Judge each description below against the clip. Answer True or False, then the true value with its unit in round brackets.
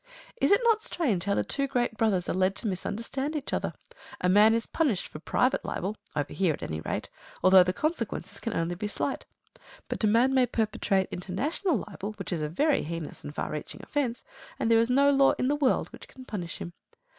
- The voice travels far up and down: True (6.7 semitones)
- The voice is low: False (220 Hz)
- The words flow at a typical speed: False (215 wpm)